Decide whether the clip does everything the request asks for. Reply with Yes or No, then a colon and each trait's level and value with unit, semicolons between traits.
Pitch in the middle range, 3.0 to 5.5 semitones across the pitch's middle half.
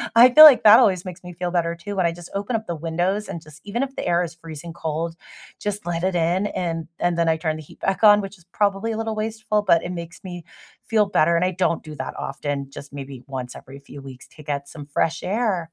Yes: medium, 175 Hz; average, 4.1 semitones